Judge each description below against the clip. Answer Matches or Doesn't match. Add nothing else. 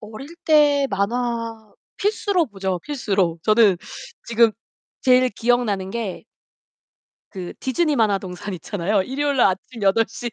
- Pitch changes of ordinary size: Matches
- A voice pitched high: Matches